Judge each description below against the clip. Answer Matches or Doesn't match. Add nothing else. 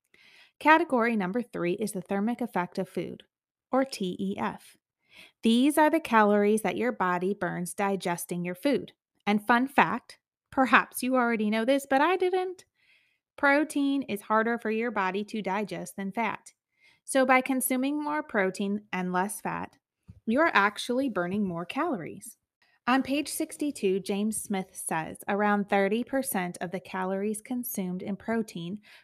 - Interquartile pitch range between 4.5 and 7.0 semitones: Matches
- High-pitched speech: Matches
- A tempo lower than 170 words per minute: Matches